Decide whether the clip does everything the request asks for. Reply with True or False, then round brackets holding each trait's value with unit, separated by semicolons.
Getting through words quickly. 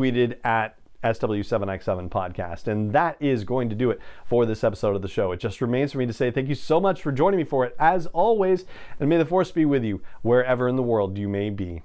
True (250 wpm)